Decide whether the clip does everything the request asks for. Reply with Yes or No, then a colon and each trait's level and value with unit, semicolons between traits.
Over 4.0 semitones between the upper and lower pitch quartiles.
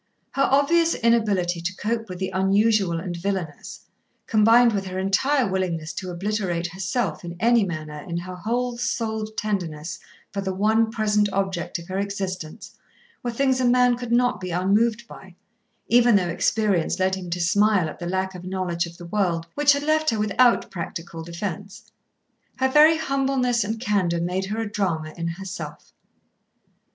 Yes: average, 4.6 semitones